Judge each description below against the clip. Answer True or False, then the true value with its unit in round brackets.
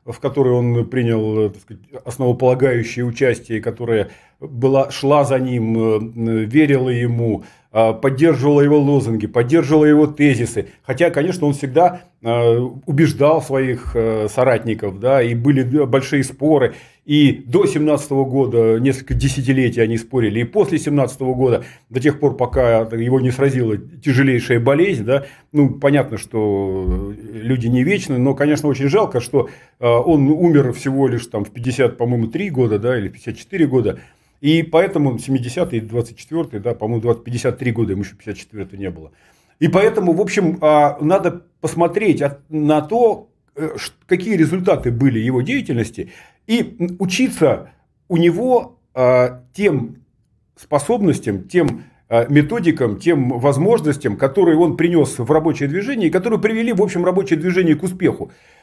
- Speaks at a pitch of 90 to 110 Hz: False (135 Hz)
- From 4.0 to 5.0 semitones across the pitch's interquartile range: True (4.7 semitones)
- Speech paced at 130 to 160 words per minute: True (135 wpm)